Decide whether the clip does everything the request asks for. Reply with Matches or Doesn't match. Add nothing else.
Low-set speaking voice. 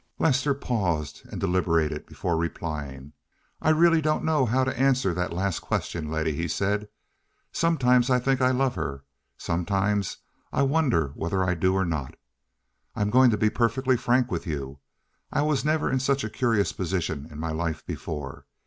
Matches